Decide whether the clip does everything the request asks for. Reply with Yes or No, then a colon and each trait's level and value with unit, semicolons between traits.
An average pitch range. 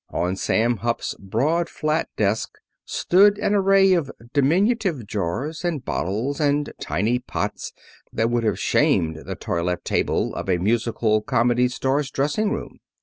No: wide, 7.0 semitones